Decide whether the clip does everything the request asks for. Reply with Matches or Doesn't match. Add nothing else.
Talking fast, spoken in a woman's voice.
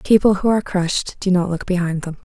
Matches